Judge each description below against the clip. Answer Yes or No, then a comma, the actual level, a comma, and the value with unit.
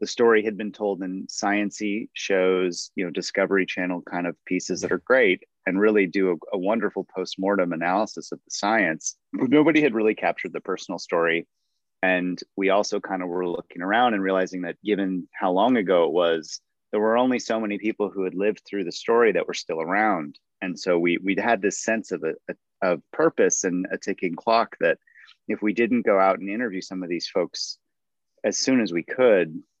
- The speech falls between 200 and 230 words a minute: Yes, fast, 205 wpm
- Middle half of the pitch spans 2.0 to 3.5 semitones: Yes, average, 2.9 semitones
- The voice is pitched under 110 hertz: Yes, very low, 95 Hz